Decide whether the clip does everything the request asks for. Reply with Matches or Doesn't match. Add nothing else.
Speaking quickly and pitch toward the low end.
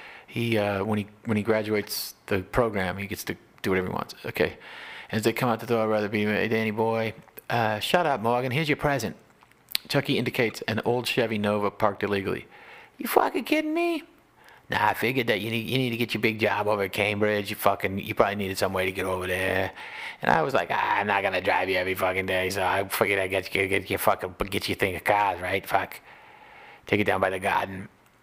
Matches